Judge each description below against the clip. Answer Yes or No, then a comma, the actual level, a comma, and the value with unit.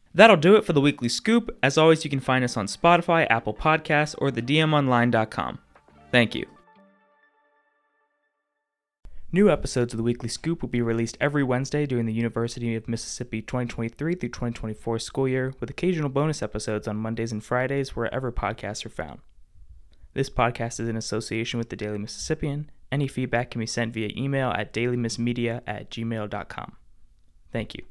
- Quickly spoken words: No, average, 165 wpm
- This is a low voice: Yes, low, 120 Hz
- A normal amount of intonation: Yes, average, 4.5 semitones